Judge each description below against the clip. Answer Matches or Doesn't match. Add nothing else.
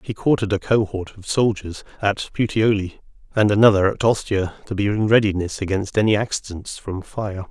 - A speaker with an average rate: Matches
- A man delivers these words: Matches